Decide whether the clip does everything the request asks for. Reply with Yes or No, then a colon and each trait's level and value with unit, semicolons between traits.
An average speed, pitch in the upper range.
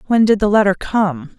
No: fast, 215 wpm; high, 205 Hz